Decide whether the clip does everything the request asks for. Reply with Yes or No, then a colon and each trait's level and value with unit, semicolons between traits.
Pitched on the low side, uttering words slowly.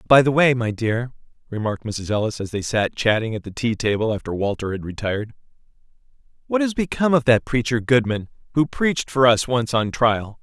No: low, 120 Hz; average, 195 wpm